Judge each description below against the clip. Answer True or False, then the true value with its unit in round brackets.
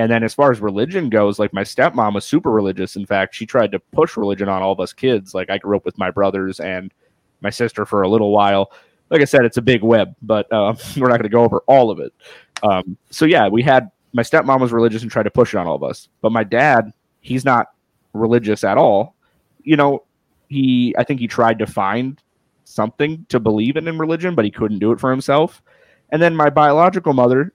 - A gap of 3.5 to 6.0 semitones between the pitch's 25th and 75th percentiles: True (4.6 semitones)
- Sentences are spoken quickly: True (240 wpm)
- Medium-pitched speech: False (115 Hz)